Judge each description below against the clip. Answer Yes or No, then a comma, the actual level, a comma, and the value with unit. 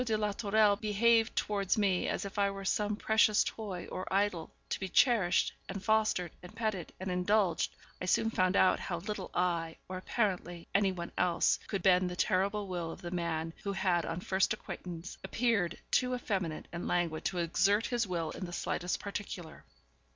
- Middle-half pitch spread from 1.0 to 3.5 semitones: Yes, average, 2.9 semitones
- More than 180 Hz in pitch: Yes, high, 190 Hz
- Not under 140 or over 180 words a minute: No, average, 190 wpm